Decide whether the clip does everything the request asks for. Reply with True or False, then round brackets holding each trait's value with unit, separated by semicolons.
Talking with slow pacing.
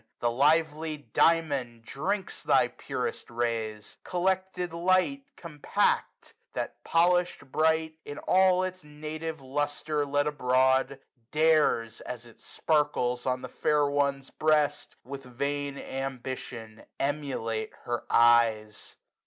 True (110 wpm)